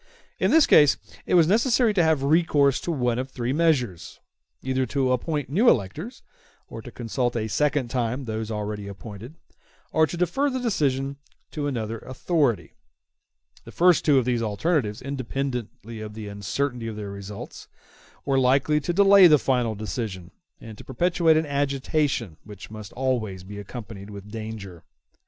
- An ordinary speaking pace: Yes, average, 160 wpm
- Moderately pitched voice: No, low, 130 Hz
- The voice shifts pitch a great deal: Yes, wide, 5.8 semitones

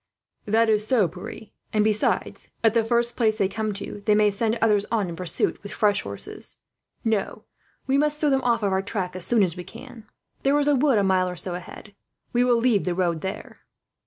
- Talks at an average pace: No, fast, 220 wpm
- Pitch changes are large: No, average, 3.7 semitones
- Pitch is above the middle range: Yes, high, 215 Hz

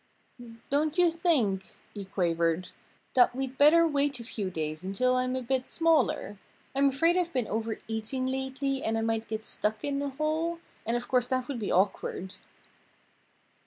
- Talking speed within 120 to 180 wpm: Yes, average, 165 wpm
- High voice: Yes, very high, 255 Hz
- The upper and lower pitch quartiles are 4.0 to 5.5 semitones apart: Yes, average, 4.7 semitones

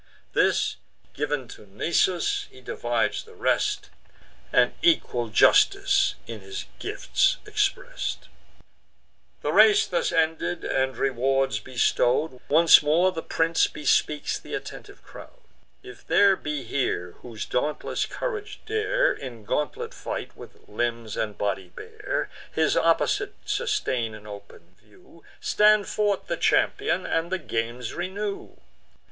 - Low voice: No, medium, 150 Hz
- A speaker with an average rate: No, slow, 125 wpm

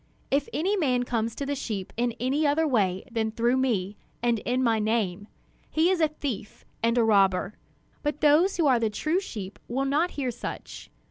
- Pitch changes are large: No, average, 5.0 semitones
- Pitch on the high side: Yes, high, 245 Hz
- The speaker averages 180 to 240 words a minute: Yes, average, 195 wpm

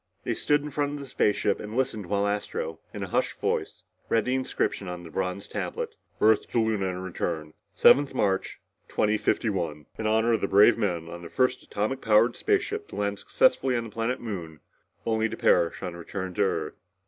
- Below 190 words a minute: No, average, 200 wpm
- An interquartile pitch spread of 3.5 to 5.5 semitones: Yes, average, 4.8 semitones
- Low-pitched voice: Yes, low, 105 Hz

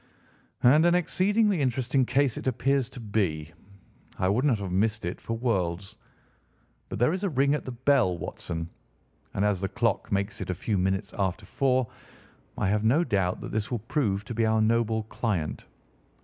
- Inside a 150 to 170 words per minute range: No, average, 185 wpm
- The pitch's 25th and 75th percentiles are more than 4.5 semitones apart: Yes, average, 5.0 semitones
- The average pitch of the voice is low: Yes, low, 110 Hz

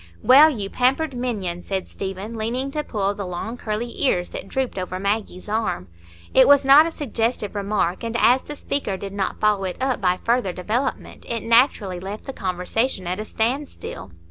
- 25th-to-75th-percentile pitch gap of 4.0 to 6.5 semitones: Yes, average, 4.9 semitones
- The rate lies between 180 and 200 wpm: Yes, average, 185 wpm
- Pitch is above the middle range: Yes, high, 215 Hz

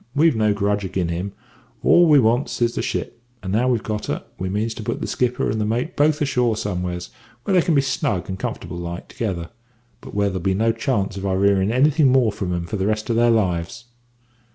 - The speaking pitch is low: Yes, low, 110 Hz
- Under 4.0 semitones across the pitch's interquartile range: No, average, 4.5 semitones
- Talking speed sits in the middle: No, fast, 230 wpm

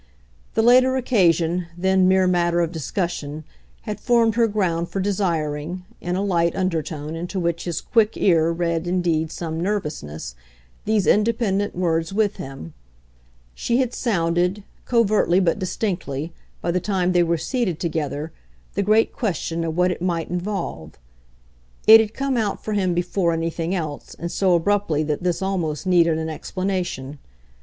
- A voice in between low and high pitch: Yes, medium, 175 Hz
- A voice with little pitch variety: No, average, 3.5 semitones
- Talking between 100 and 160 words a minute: Yes, average, 155 wpm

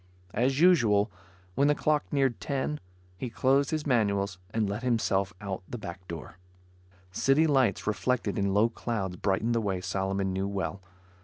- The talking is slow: No, average, 160 wpm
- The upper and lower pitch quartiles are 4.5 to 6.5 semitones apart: Yes, average, 5.2 semitones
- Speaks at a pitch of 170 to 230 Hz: No, low, 105 Hz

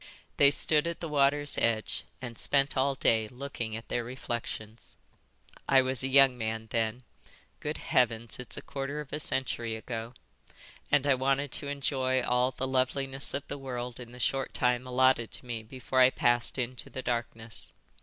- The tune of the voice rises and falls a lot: No, narrow, 2.5 semitones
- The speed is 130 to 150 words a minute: No, average, 170 wpm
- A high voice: No, low, 130 Hz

